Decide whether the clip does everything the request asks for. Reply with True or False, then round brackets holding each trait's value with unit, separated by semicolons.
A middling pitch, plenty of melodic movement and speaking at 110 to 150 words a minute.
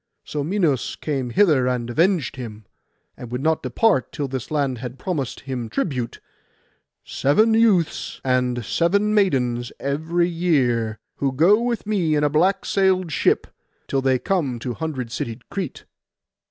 True (145 Hz; 6.1 semitones; 145 wpm)